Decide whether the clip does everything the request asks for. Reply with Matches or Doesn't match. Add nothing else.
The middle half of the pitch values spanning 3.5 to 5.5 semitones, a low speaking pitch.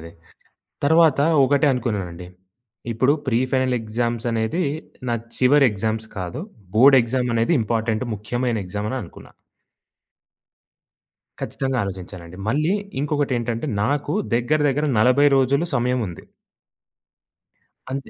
Matches